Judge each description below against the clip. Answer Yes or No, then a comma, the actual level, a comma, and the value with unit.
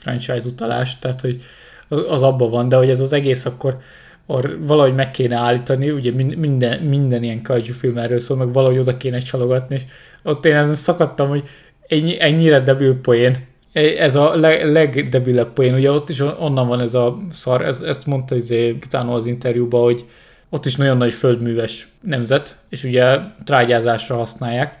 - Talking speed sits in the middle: No, fast, 165 wpm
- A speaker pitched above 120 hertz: Yes, low, 130 Hz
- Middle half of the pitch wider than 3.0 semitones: No, average, 2.7 semitones